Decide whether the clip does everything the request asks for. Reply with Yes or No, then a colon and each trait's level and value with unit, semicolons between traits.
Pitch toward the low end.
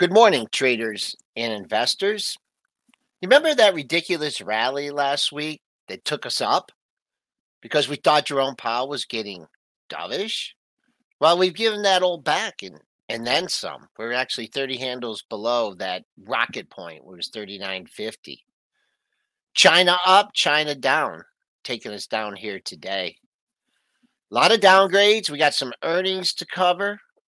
No: medium, 175 Hz